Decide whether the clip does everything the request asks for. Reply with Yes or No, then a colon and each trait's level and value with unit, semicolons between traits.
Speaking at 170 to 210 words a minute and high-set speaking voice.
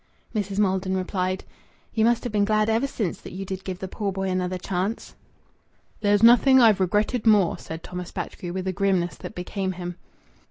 Yes: average, 190 wpm; high, 195 Hz